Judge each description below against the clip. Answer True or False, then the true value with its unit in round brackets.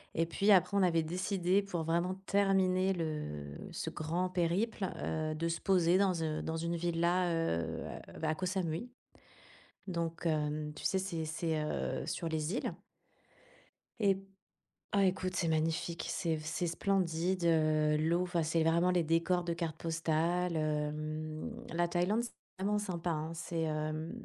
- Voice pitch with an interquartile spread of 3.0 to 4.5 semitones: False (2.6 semitones)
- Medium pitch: True (170 Hz)